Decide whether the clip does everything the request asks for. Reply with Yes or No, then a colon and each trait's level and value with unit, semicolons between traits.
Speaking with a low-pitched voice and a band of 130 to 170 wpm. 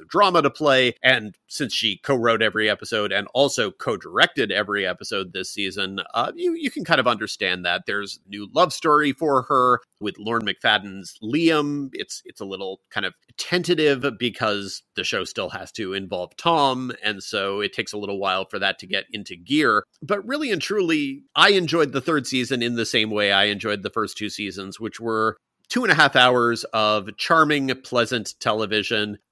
No: low, 120 Hz; average, 190 wpm